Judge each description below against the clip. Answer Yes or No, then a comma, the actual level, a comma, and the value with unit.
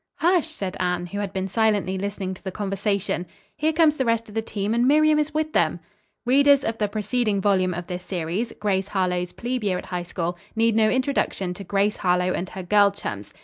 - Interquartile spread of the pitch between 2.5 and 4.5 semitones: Yes, average, 4.0 semitones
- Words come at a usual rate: No, fast, 215 wpm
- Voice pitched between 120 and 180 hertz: No, high, 205 Hz